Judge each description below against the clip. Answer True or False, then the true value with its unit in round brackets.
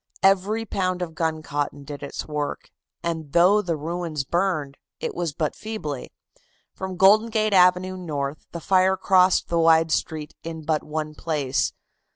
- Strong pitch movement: False (3.5 semitones)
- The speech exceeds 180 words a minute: False (155 wpm)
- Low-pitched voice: False (165 Hz)